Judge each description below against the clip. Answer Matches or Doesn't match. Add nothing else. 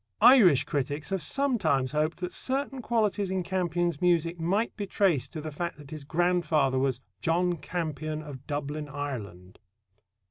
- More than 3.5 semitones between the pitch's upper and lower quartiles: Matches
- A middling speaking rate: Matches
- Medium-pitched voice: Matches